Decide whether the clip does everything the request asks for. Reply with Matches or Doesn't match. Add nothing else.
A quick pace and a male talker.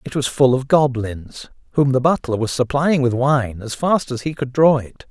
Matches